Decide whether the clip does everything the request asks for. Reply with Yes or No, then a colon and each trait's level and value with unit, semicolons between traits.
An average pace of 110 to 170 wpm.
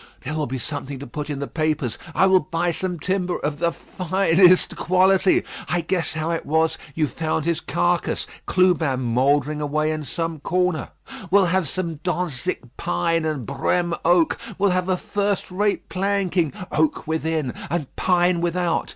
Yes: average, 165 wpm